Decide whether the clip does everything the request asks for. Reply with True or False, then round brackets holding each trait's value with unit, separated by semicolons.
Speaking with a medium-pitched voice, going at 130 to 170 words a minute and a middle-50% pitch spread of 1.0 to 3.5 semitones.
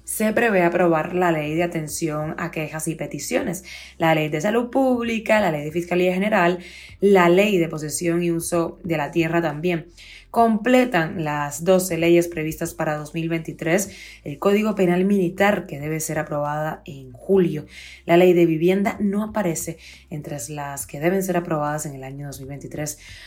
True (170 Hz; 165 wpm; 2.9 semitones)